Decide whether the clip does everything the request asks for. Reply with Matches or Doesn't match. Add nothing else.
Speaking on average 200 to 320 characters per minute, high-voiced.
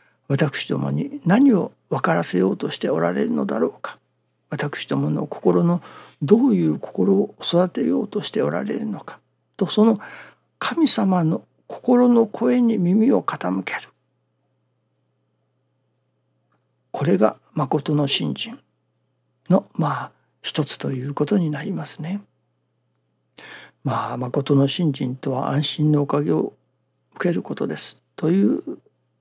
Doesn't match